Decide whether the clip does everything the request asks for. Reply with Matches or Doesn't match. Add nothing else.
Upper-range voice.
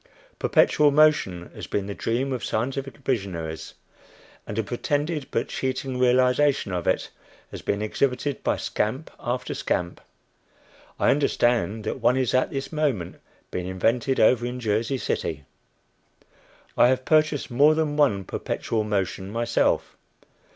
Doesn't match